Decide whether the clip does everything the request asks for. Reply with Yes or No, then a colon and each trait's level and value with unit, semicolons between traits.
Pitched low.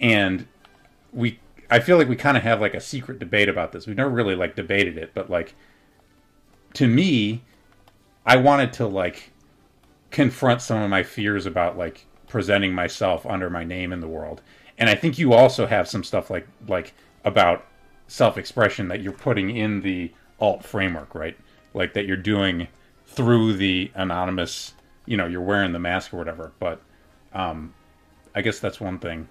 Yes: low, 100 Hz